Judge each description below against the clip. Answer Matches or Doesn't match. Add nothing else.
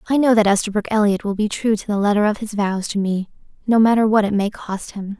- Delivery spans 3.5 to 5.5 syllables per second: Doesn't match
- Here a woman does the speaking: Matches